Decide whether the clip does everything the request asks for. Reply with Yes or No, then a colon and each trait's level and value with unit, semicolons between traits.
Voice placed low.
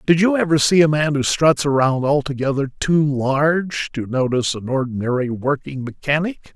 No: medium, 145 Hz